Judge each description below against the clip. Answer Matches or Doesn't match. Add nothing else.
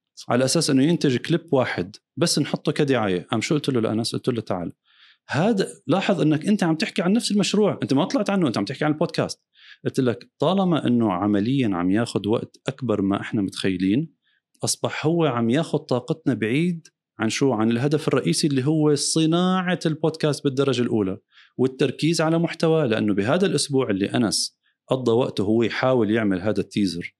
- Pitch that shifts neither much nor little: Doesn't match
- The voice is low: Doesn't match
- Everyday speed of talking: Doesn't match